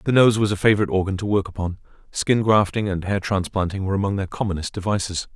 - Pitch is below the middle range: Yes, low, 100 Hz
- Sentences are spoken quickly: Yes, fast, 215 wpm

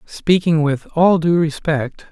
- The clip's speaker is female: No, male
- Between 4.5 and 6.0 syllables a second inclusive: No, 3.7 syllables/s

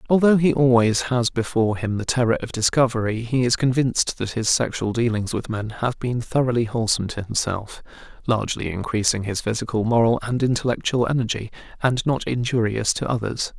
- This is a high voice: No, low, 115 Hz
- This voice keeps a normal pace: Yes, average, 170 wpm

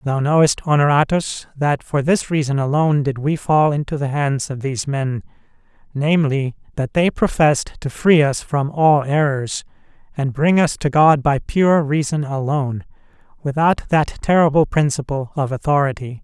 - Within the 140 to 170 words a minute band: Yes, average, 150 wpm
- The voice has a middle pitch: Yes, medium, 145 Hz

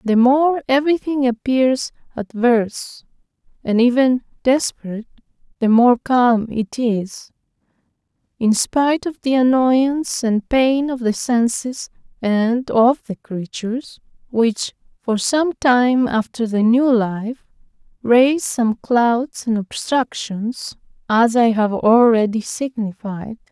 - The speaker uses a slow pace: Yes, slow, 115 wpm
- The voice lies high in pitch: Yes, high, 240 Hz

